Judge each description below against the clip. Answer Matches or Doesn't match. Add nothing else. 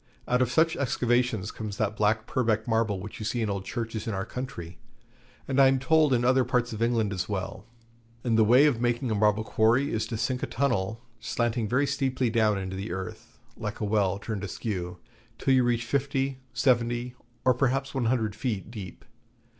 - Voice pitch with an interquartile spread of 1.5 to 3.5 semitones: Matches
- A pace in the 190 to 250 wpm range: Matches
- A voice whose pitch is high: Doesn't match